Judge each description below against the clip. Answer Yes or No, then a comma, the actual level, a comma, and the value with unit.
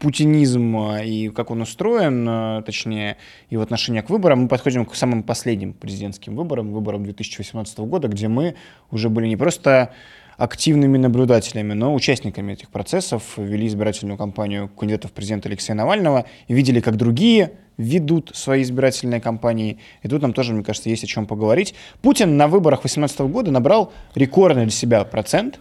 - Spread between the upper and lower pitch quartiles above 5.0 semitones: No, average, 4.0 semitones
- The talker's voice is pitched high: No, low, 115 Hz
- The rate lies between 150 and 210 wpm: Yes, fast, 160 wpm